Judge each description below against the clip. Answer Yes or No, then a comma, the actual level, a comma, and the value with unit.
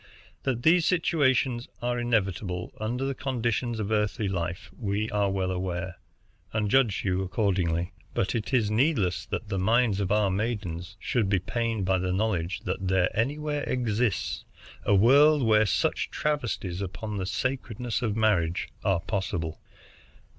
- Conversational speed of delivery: Yes, average, 150 wpm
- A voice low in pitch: Yes, low, 105 Hz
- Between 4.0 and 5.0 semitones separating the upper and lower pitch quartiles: Yes, average, 4.3 semitones